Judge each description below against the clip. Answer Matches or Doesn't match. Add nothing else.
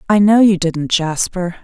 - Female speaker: Matches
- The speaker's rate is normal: Matches